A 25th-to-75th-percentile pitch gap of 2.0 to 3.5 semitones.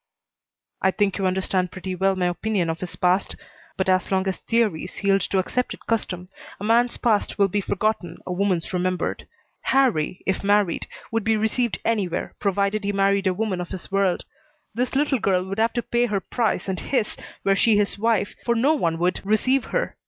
Yes: average, 3.2 semitones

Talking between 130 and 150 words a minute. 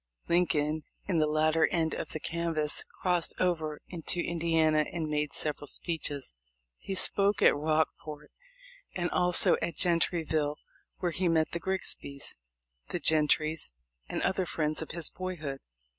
Yes: average, 140 wpm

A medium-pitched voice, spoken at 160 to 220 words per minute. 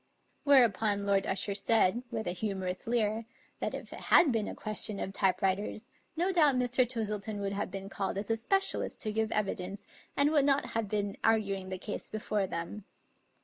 No: high, 210 Hz; average, 190 wpm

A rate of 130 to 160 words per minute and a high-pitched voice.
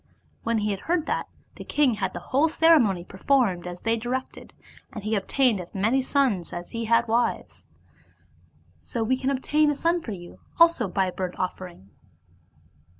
No: average, 170 wpm; high, 230 Hz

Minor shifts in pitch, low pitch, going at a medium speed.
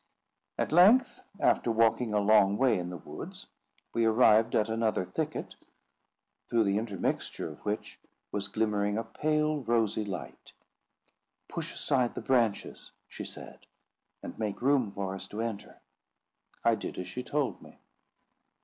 No: average, 3.1 semitones; low, 110 Hz; average, 145 wpm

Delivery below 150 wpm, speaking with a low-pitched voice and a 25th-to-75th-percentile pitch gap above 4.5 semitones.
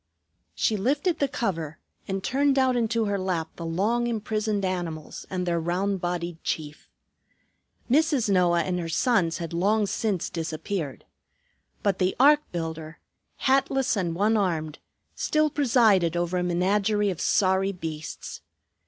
No: average, 140 wpm; high, 190 Hz; average, 4.9 semitones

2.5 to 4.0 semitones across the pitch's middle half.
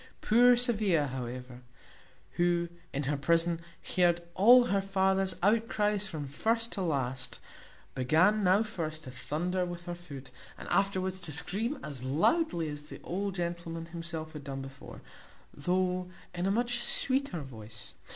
No: average, 5.1 semitones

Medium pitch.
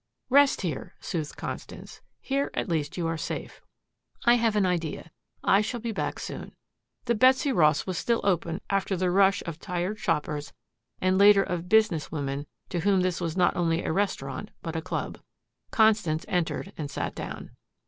Yes: medium, 180 Hz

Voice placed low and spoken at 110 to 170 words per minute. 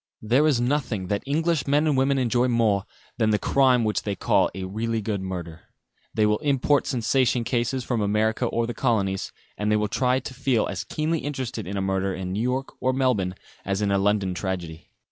No: low, 115 Hz; average, 200 wpm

